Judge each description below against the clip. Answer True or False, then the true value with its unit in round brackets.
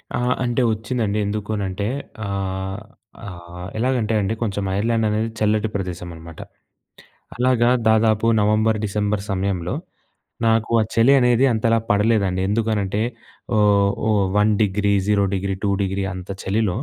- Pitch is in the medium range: False (105 Hz)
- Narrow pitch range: True (2.3 semitones)